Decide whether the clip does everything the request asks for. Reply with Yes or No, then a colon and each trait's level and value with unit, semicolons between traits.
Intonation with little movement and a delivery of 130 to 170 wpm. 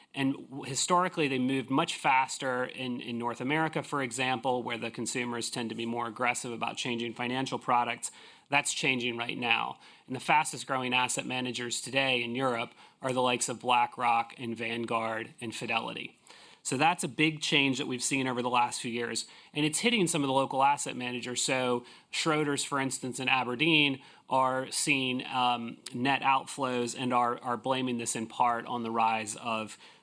No: narrow, 2.1 semitones; average, 180 wpm